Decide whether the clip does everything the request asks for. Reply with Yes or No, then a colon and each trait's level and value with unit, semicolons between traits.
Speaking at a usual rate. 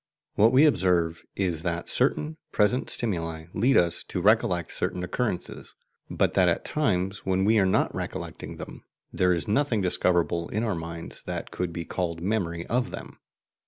Yes: average, 165 wpm